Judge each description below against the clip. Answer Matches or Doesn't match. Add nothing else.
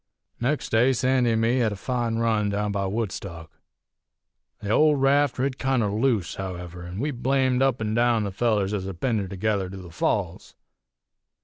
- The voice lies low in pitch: Matches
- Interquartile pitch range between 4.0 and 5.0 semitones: Matches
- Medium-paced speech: Matches